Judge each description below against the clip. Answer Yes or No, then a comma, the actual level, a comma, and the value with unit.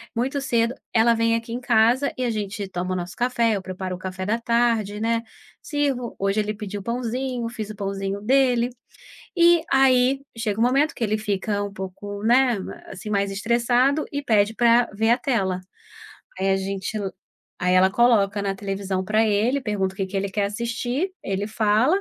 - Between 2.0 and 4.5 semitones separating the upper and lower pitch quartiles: Yes, average, 3.5 semitones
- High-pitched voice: Yes, high, 220 Hz